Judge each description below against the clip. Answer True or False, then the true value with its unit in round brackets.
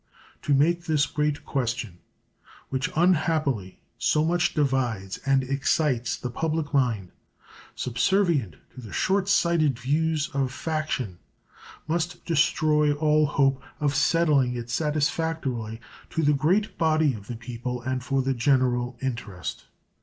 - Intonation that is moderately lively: True (4.1 semitones)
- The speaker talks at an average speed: False (130 wpm)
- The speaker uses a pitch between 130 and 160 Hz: True (140 Hz)